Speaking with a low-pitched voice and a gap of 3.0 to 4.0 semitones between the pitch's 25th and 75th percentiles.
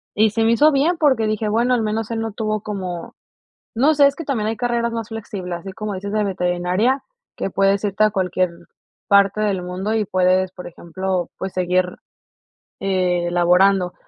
No: high, 200 Hz; average, 3.4 semitones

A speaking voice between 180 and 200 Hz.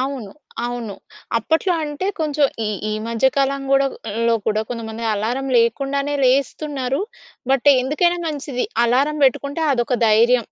No: very high, 270 Hz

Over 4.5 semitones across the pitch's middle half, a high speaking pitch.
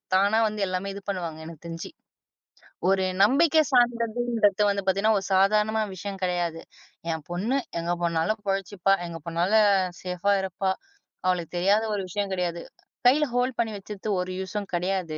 No: average, 3.3 semitones; high, 195 Hz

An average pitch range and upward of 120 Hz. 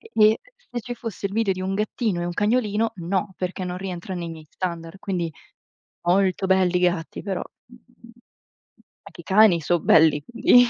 Yes: average, 3.6 semitones; high, 190 Hz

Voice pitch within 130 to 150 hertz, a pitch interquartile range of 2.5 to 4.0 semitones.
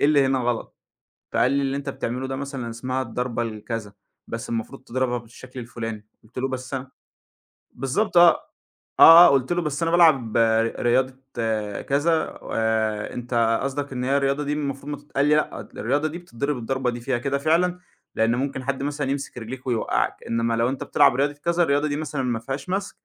Yes: low, 135 Hz; average, 3.3 semitones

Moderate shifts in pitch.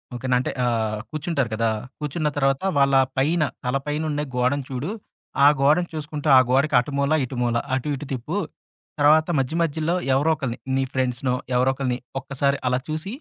Yes: average, 3.3 semitones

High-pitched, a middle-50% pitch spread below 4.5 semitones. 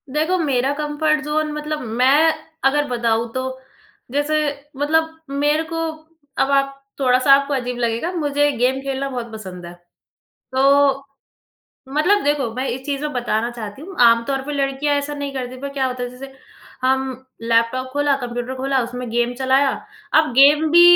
Yes: very high, 275 Hz; average, 2.9 semitones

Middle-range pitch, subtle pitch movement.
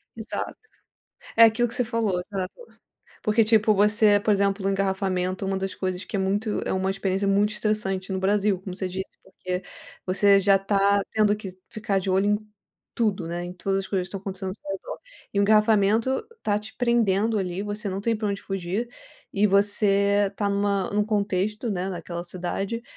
No: high, 200 Hz; narrow, 1.8 semitones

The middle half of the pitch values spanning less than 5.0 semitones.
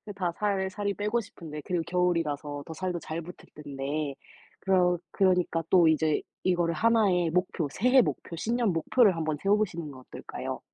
Yes: average, 3.7 semitones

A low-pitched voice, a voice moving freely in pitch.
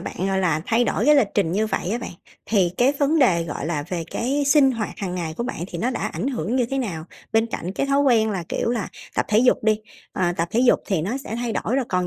No: high, 220 Hz; wide, 5.7 semitones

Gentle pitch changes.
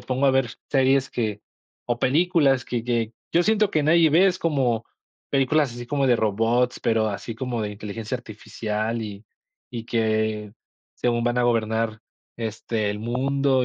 No: average, 3.4 semitones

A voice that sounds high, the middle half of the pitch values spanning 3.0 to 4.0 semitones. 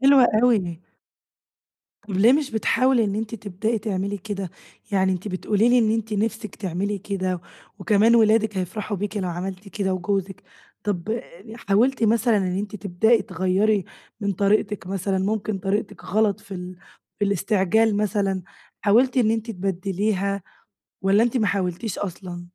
No: high, 205 Hz; narrow, 2.5 semitones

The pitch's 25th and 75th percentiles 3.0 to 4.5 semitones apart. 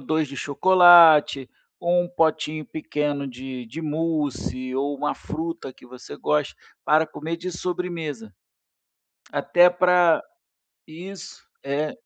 Yes: average, 3.6 semitones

